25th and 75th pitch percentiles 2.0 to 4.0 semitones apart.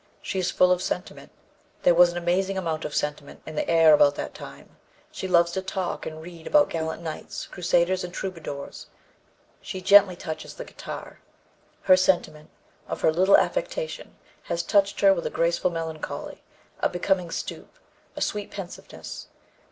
Yes: narrow, 2.6 semitones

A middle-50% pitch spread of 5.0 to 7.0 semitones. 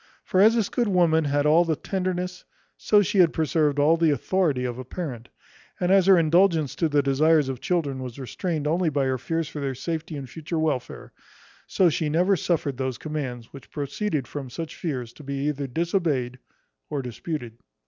No: average, 4.2 semitones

